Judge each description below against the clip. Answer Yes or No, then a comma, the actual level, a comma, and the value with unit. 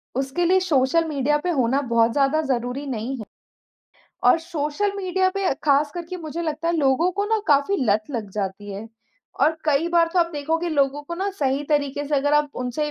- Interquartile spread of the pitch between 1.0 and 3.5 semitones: No, average, 4.1 semitones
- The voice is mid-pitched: No, very high, 295 Hz